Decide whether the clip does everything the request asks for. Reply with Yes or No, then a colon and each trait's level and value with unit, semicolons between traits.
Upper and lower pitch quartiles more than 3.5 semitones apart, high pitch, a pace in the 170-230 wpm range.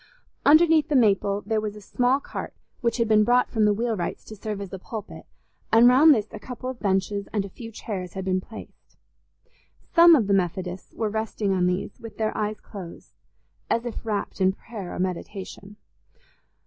No: average, 3.1 semitones; high, 215 Hz; average, 190 wpm